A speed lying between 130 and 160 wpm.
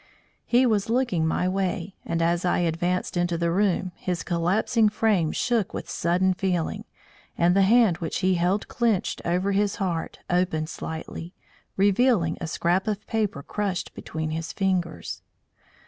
Yes: average, 150 wpm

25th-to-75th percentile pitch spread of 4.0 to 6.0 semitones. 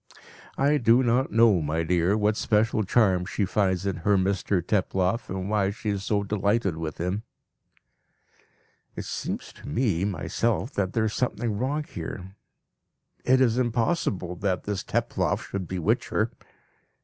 No: average, 3.6 semitones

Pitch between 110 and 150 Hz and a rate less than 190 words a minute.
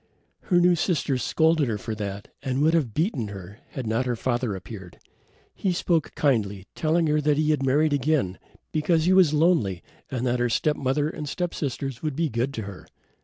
No: medium, 140 Hz; average, 195 wpm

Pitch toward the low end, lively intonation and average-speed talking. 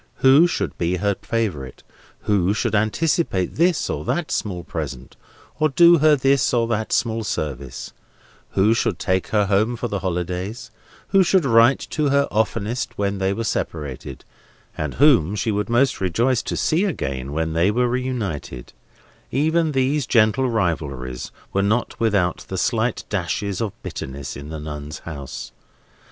Yes: low, 105 Hz; wide, 7.2 semitones; average, 160 wpm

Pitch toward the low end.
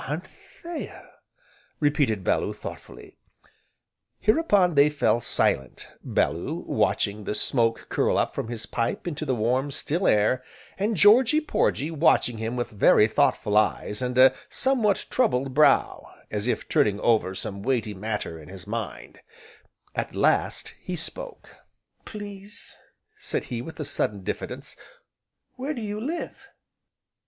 Yes: low, 130 Hz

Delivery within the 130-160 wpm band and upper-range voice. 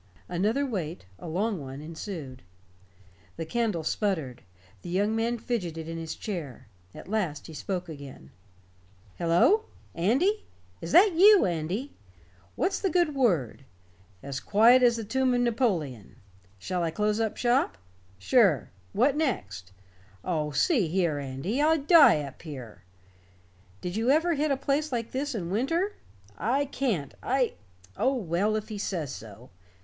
Yes: average, 145 wpm; high, 205 Hz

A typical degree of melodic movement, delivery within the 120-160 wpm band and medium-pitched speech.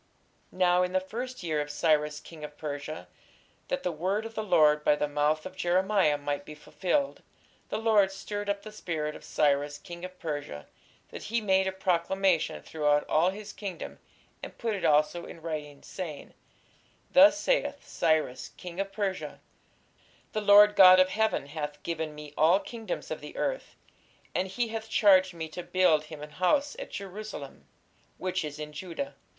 No: average, 5.0 semitones; average, 175 wpm; medium, 180 Hz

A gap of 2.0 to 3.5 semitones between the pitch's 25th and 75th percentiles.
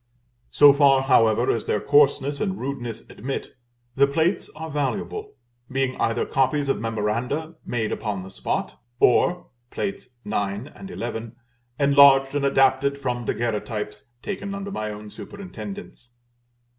No: average, 4.4 semitones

